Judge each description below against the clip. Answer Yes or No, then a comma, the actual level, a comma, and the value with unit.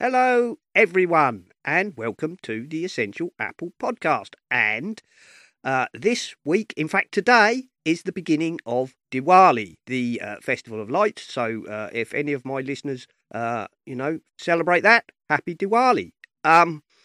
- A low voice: No, medium, 165 Hz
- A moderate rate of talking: Yes, average, 145 wpm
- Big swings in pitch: Yes, wide, 7.1 semitones